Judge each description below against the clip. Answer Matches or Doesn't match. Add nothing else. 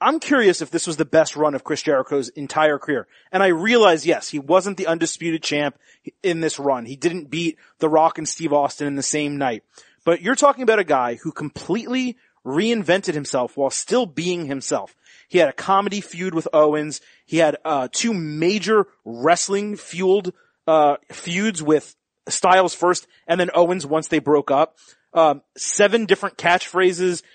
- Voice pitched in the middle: Matches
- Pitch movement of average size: Matches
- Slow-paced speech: Doesn't match